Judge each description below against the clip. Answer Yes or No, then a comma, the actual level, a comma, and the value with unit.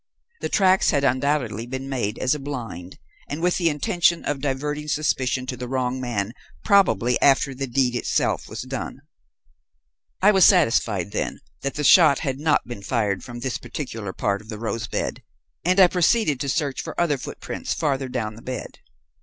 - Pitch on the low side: Yes, low, 130 Hz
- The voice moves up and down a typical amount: Yes, average, 4.0 semitones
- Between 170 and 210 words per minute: Yes, average, 180 wpm